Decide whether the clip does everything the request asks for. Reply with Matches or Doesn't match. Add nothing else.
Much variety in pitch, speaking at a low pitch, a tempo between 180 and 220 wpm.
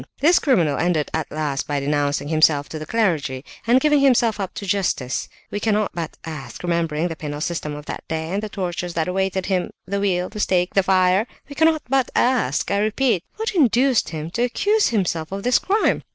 Doesn't match